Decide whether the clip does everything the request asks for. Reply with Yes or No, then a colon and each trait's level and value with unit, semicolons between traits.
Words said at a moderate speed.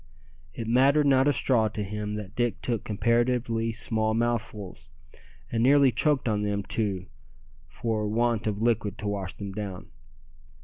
Yes: average, 150 wpm